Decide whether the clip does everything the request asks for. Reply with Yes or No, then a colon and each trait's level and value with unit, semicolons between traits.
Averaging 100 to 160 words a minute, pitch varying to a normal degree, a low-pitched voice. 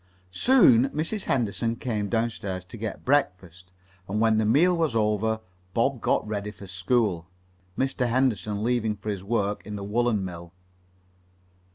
Yes: average, 150 wpm; average, 3.3 semitones; low, 110 Hz